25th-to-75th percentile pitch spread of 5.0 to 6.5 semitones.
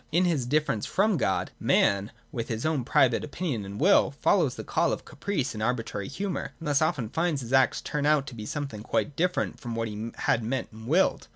Yes: wide, 5.5 semitones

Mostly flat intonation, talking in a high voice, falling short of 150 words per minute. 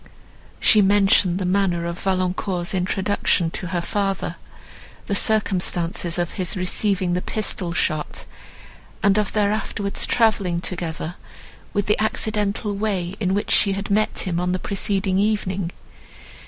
Yes: narrow, 2.3 semitones; high, 195 Hz; average, 140 wpm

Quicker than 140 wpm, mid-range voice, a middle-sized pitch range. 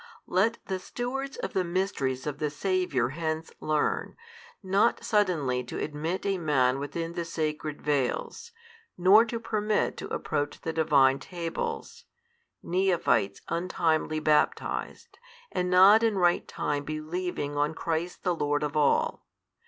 No: slow, 135 wpm; medium, 165 Hz; average, 4.2 semitones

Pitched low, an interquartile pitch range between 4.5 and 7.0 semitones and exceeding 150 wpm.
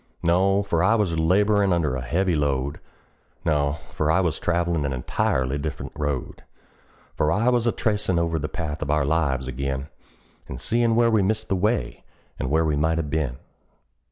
Yes: very low, 80 Hz; average, 5.1 semitones; average, 185 wpm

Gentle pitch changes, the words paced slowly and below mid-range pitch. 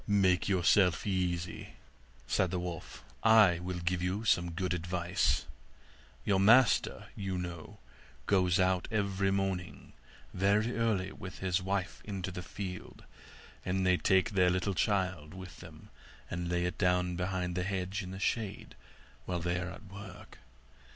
No: narrow, 1.7 semitones; average, 150 wpm; very low, 90 Hz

